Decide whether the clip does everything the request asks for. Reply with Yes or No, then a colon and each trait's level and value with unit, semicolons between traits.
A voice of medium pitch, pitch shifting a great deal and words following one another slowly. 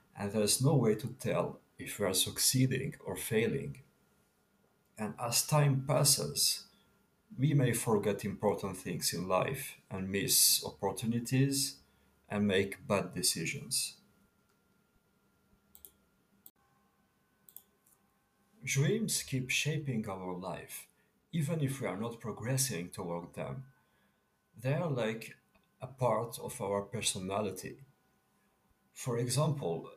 No: low, 115 Hz; wide, 6.0 semitones; slow, 110 wpm